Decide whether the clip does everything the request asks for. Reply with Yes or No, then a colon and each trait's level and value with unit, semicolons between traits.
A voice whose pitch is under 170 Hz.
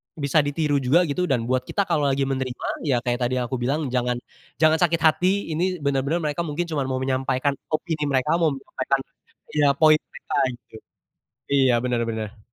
Yes: medium, 140 Hz